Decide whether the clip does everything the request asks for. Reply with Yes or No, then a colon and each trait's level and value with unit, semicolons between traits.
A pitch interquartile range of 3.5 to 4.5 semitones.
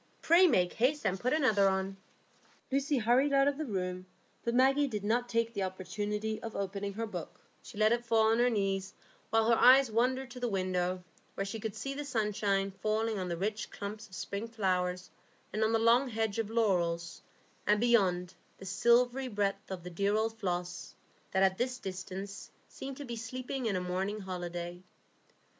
Yes: average, 3.9 semitones